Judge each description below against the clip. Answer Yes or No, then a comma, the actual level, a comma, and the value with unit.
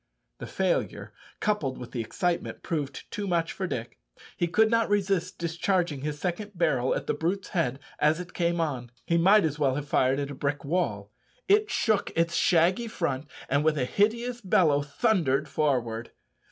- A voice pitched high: No, medium, 165 Hz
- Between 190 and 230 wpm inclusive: No, average, 180 wpm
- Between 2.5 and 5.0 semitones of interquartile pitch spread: No, wide, 5.5 semitones